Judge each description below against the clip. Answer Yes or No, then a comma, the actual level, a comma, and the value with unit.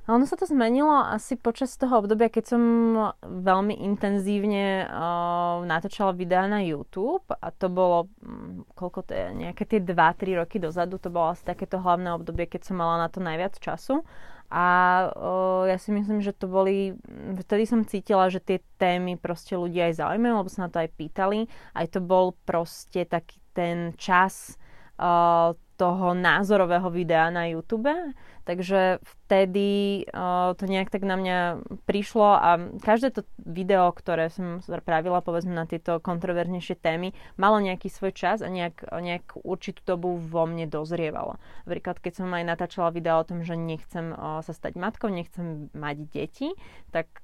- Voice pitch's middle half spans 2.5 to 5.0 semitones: Yes, average, 2.9 semitones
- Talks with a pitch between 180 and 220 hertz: Yes, medium, 185 Hz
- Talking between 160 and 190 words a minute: Yes, fast, 165 wpm